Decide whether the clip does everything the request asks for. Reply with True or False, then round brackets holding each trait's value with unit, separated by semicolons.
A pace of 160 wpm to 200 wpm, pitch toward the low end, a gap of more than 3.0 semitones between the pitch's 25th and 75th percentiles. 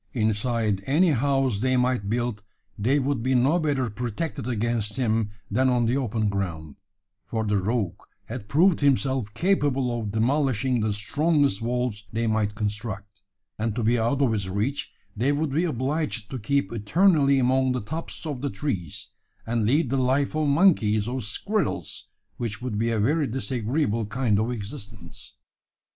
True (165 wpm; 120 Hz; 4.4 semitones)